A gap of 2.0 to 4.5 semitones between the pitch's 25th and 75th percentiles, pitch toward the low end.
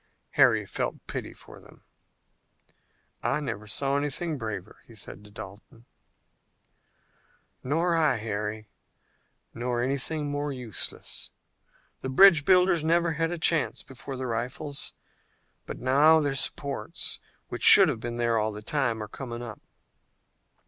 No: average, 5.2 semitones; low, 130 Hz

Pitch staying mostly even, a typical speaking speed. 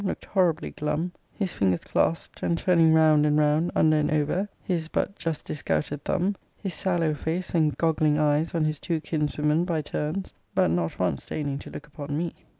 Yes: narrow, 2.3 semitones; average, 185 wpm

